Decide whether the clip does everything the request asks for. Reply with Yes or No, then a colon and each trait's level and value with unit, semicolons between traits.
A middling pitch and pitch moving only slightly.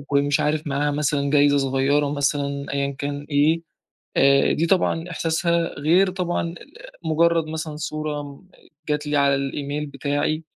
Yes: medium, 145 Hz; narrow, 2.1 semitones